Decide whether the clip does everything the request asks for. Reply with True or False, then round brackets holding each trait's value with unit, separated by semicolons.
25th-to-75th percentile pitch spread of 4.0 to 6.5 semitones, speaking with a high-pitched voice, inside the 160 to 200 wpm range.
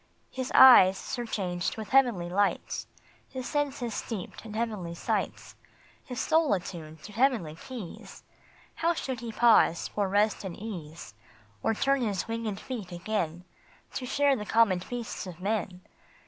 False (5.2 semitones; 215 Hz; 145 wpm)